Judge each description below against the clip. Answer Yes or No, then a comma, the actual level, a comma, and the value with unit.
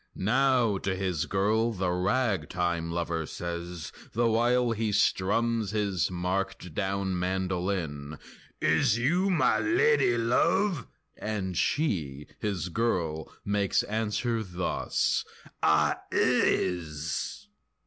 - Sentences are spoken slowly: Yes, slow, 100 wpm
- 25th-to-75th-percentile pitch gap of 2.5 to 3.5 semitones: No, average, 4.7 semitones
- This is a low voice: Yes, very low, 95 Hz